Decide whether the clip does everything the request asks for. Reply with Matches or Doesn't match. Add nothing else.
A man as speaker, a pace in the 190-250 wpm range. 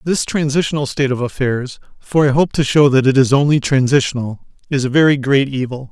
Matches